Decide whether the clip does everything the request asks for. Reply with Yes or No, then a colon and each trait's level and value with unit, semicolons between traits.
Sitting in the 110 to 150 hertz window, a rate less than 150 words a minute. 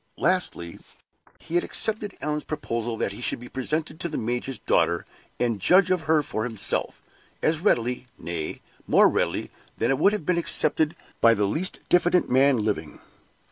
No: low, 135 Hz; average, 170 wpm